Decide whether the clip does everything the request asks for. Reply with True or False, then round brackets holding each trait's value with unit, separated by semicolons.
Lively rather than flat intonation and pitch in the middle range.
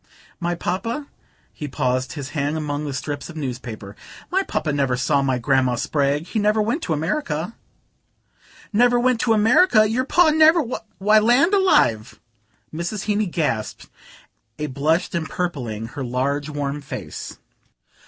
True (7.8 semitones; 155 Hz)